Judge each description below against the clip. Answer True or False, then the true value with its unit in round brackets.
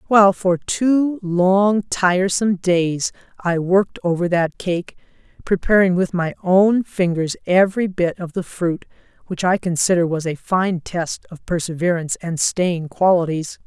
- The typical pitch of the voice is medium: True (180 Hz)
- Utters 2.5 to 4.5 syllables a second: True (4.3 syllables/s)